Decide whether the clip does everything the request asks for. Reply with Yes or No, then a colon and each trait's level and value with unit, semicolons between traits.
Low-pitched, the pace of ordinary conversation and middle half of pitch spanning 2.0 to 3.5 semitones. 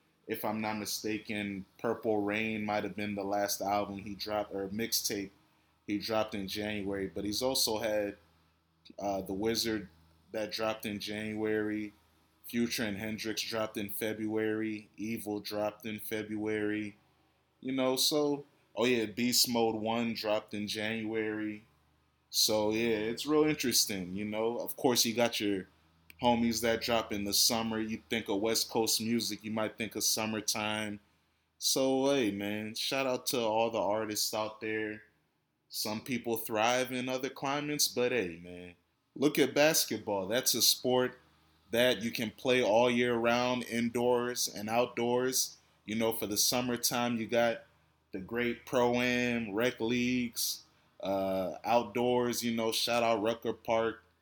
Yes: low, 110 Hz; average, 155 wpm; narrow, 2.5 semitones